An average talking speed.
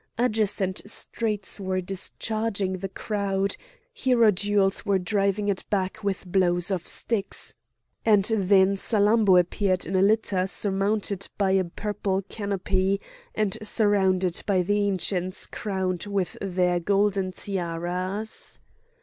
No: slow, 115 wpm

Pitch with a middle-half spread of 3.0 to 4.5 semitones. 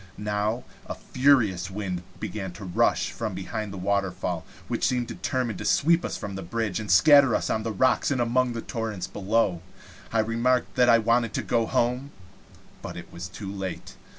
Yes: average, 4.0 semitones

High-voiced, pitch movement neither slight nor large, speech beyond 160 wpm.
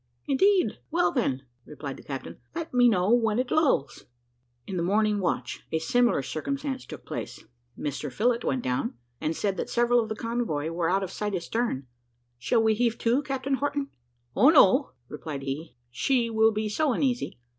No: high, 220 Hz; wide, 7.1 semitones; average, 175 wpm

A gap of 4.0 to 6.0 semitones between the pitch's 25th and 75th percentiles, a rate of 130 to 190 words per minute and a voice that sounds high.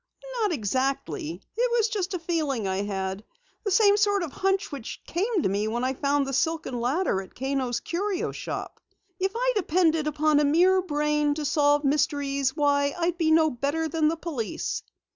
Yes: average, 4.7 semitones; average, 180 wpm; very high, 300 Hz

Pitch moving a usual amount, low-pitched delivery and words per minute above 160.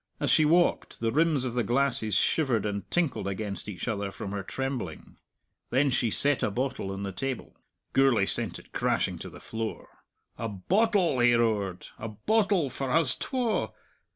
No: wide, 5.8 semitones; low, 120 Hz; average, 175 wpm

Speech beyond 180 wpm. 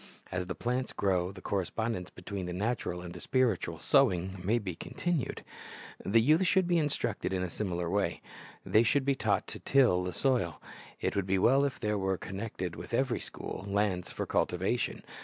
Yes: average, 190 wpm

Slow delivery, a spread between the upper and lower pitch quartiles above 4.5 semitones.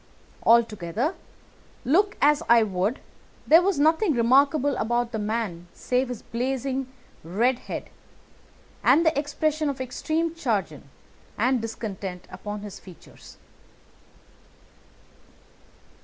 Yes: slow, 105 wpm; wide, 5.4 semitones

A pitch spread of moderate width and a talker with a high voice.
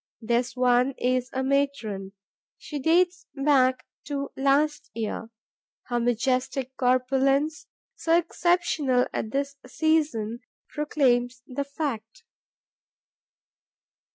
Yes: average, 3.1 semitones; very high, 265 Hz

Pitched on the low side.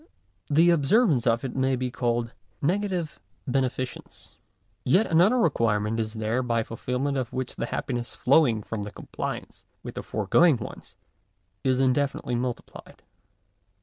Yes: low, 130 Hz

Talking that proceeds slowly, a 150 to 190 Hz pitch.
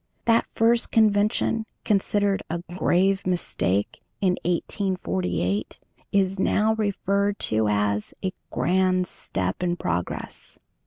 Yes: slow, 105 wpm; medium, 185 Hz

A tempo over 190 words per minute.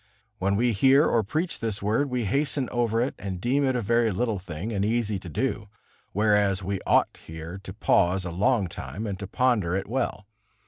Yes: average, 200 wpm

